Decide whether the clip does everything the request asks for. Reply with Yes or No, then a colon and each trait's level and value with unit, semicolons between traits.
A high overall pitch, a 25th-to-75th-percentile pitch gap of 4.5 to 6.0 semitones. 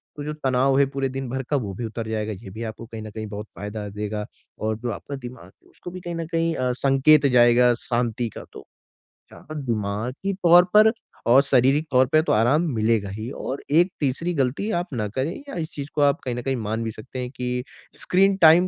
No: low, 125 Hz; average, 5.1 semitones